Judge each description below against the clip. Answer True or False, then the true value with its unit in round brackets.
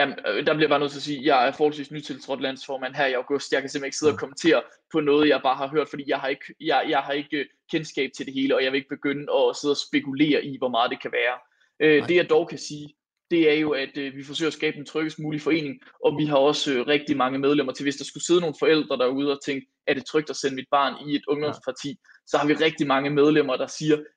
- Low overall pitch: False (145 Hz)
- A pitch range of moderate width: False (1.8 semitones)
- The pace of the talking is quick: True (270 wpm)